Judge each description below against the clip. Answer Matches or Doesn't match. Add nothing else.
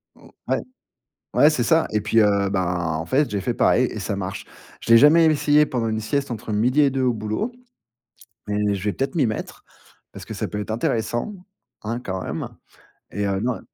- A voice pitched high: Doesn't match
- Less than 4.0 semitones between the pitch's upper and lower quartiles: Doesn't match